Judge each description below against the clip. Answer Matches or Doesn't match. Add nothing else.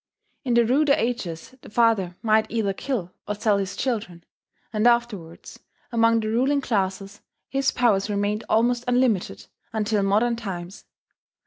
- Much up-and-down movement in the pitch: Doesn't match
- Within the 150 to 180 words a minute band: Doesn't match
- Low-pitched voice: Doesn't match